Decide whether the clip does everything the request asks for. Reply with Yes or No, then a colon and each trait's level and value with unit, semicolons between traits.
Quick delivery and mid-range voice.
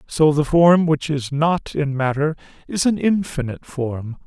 No: average, 170 wpm; medium, 150 Hz